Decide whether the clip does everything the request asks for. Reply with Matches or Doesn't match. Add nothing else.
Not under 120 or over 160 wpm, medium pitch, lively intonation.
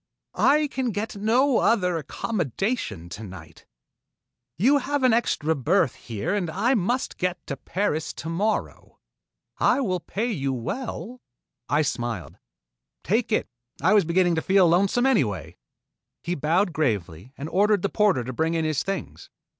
Matches